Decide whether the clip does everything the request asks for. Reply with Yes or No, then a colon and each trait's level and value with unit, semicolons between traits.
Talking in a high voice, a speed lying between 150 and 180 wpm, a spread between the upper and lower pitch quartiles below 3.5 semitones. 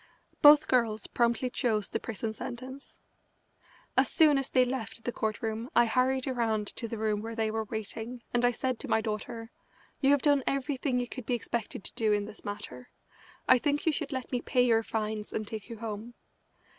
No: high, 235 Hz; fast, 205 wpm; average, 2.7 semitones